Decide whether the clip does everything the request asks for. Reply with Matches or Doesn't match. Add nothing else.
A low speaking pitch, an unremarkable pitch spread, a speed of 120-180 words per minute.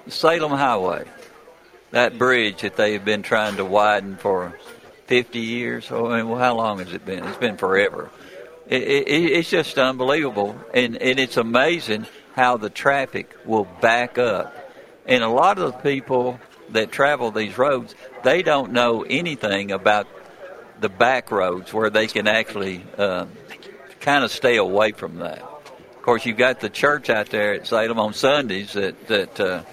Matches